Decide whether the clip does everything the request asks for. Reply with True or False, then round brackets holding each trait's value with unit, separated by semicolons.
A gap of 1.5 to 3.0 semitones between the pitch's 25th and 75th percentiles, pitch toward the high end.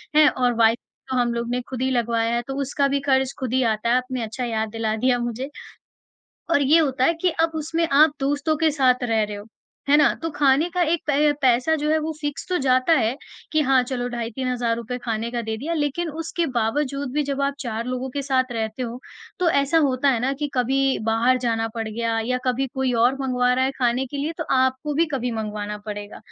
False (3.4 semitones; 255 Hz)